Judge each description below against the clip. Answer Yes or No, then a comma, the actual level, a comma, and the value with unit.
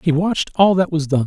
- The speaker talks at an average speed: No, fast, 285 wpm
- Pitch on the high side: No, medium, 165 Hz